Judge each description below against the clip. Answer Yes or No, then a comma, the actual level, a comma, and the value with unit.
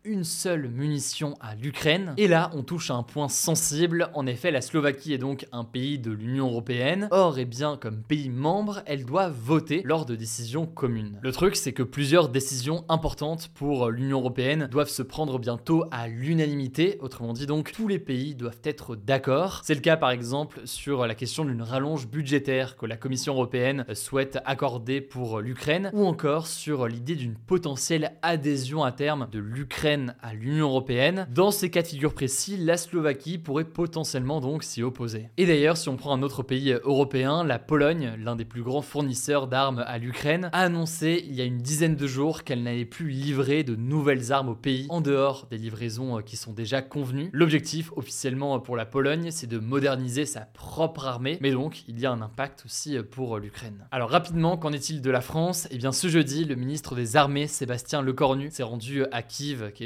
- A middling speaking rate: Yes, average, 200 wpm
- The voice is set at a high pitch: No, medium, 140 Hz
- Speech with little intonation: No, average, 3.5 semitones